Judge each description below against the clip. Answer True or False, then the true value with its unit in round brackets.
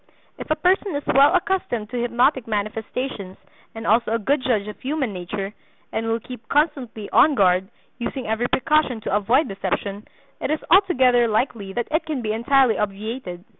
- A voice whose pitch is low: False (235 Hz)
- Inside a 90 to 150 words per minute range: False (170 wpm)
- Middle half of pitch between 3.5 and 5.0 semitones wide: True (4.6 semitones)